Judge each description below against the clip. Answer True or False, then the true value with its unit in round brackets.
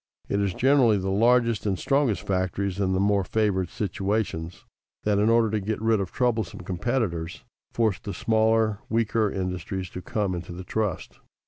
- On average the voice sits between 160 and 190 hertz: False (100 Hz)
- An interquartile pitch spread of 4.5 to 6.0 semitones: False (3.2 semitones)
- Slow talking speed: False (165 wpm)